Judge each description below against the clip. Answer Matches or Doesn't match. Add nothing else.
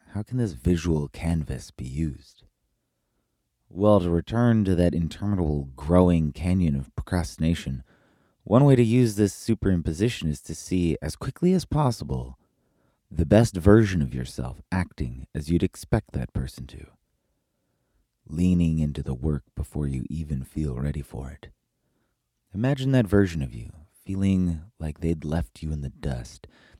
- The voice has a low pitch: Matches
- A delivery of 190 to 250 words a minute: Doesn't match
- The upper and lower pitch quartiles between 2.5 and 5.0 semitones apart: Doesn't match